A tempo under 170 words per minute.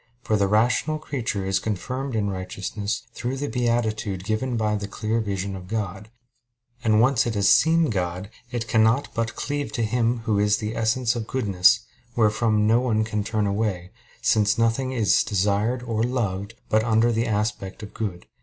No: average, 180 wpm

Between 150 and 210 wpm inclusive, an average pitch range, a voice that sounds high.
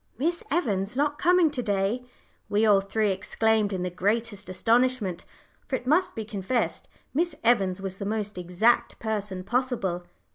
Yes: average, 155 wpm; average, 4.5 semitones; high, 215 Hz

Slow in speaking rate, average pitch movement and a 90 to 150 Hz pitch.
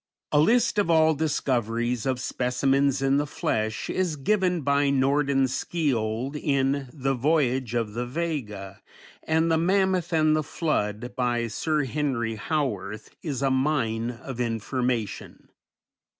Yes: slow, 130 wpm; average, 4.3 semitones; low, 135 Hz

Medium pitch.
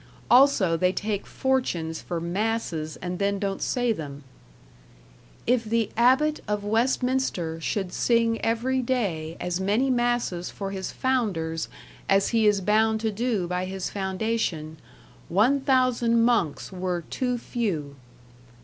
No: high, 210 Hz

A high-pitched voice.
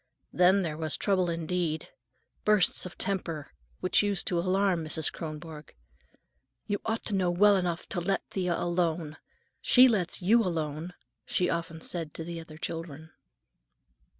No: medium, 175 Hz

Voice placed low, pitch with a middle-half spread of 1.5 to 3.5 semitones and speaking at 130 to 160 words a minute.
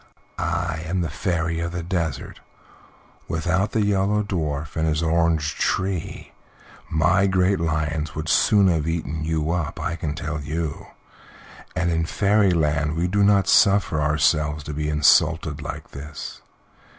Yes: very low, 80 Hz; average, 2.9 semitones; average, 145 wpm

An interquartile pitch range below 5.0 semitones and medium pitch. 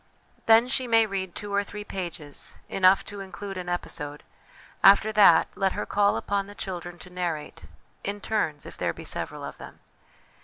No: narrow, 2.6 semitones; high, 195 Hz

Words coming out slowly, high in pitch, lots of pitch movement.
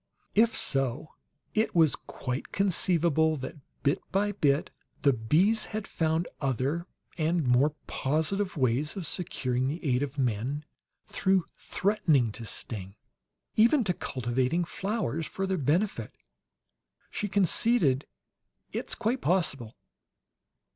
No: slow, 120 wpm; medium, 155 Hz; wide, 6.3 semitones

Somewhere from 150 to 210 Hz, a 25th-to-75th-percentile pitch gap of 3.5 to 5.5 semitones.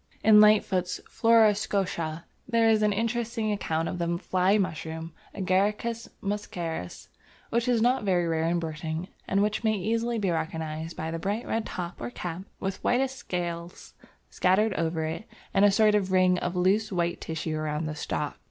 Yes: medium, 185 Hz; average, 4.4 semitones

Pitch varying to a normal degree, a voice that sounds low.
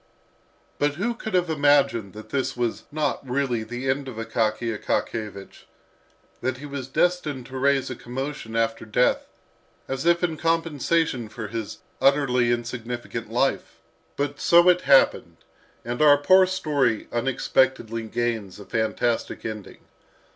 Yes: average, 4.1 semitones; low, 130 Hz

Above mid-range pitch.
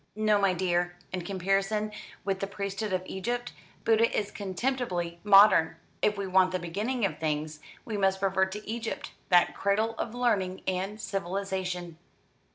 Yes: high, 195 Hz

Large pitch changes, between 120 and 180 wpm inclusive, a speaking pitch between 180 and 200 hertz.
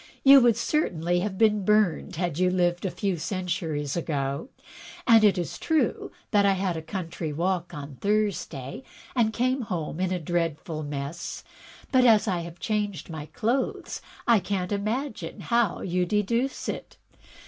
No: average, 4.3 semitones; average, 160 wpm; medium, 185 Hz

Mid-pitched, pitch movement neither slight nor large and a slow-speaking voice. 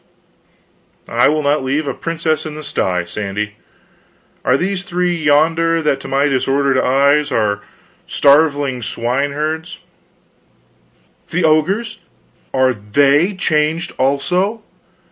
Yes: medium, 145 Hz; average, 3.6 semitones; slow, 120 wpm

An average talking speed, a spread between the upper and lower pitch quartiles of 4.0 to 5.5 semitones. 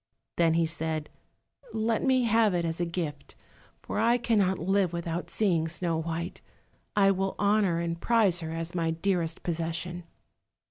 No: average, 155 wpm; average, 3.4 semitones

